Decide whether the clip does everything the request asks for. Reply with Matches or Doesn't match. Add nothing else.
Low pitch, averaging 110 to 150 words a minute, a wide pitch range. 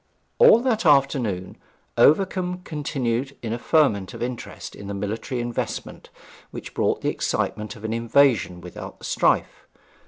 Matches